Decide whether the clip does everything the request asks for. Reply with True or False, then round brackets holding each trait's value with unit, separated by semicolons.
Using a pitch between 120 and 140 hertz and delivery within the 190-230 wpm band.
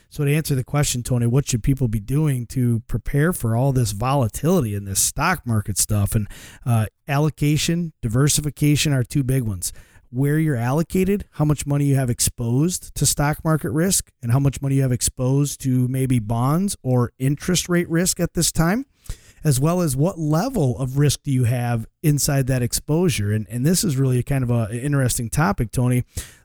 True (135 Hz; 195 wpm)